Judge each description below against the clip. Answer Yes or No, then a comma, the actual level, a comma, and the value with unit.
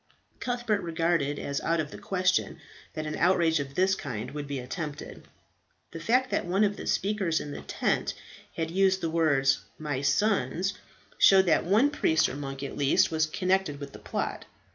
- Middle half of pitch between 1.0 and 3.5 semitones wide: No, average, 4.9 semitones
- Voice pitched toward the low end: No, medium, 165 Hz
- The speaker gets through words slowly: No, average, 185 wpm